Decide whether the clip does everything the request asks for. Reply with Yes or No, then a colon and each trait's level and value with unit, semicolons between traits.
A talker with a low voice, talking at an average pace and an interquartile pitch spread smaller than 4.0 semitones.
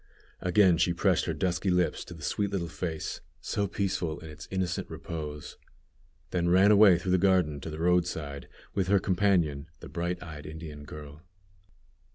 Yes: very low, 85 Hz; average, 170 wpm; average, 3.2 semitones